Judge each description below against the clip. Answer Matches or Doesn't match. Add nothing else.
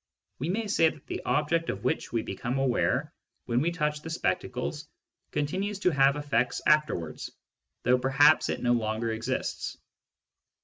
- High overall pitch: Doesn't match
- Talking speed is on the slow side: Doesn't match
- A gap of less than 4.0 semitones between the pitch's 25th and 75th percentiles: Doesn't match